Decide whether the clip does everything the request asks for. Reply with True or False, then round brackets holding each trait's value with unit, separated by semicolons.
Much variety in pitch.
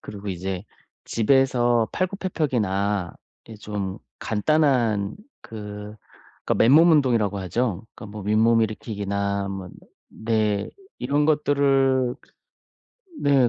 False (4.6 semitones)